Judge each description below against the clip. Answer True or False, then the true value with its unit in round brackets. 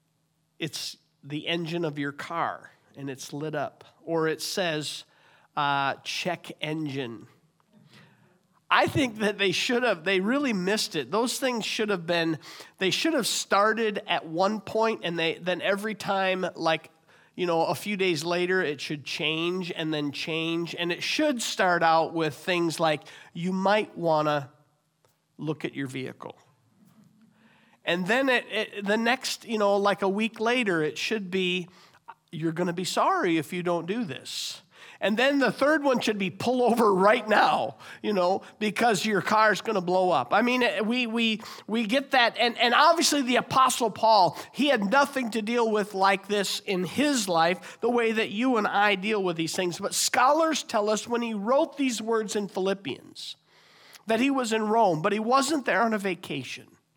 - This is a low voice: False (195 Hz)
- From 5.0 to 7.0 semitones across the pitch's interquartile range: True (5.4 semitones)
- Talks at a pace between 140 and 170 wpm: False (185 wpm)